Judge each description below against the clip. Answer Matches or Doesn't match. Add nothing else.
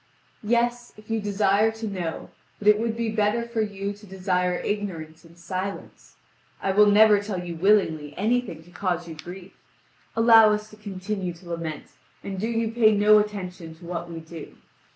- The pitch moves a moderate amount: Matches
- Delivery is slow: Doesn't match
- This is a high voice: Matches